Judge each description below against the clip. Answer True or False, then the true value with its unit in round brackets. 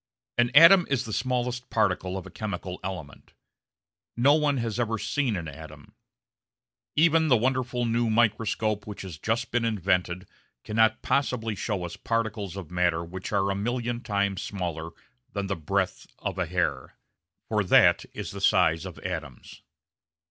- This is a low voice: True (105 Hz)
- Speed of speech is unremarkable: True (155 wpm)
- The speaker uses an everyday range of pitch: True (4.7 semitones)